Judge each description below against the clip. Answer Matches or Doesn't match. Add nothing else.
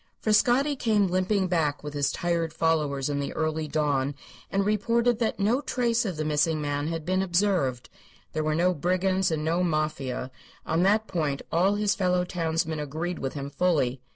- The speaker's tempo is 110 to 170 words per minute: Doesn't match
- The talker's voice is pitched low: Doesn't match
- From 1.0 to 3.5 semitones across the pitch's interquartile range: Doesn't match